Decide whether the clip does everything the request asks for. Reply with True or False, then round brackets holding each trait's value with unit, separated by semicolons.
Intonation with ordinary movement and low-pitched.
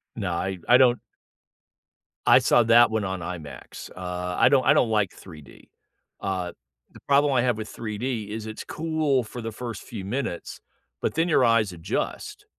True (4.8 semitones; 110 Hz)